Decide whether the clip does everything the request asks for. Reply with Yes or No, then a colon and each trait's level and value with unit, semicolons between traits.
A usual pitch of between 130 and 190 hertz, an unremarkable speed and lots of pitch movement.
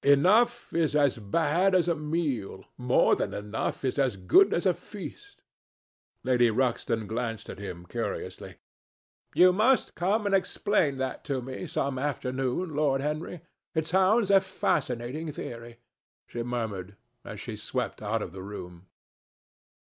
Yes: medium, 140 Hz; average, 145 wpm; wide, 7.2 semitones